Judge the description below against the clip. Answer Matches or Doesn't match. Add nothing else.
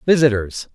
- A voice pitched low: Matches